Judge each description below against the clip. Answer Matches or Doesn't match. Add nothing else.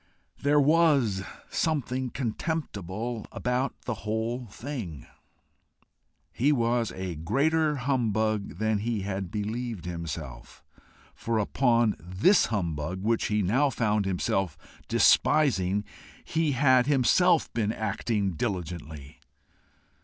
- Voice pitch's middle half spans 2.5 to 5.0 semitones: Doesn't match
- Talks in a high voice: Doesn't match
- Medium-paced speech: Doesn't match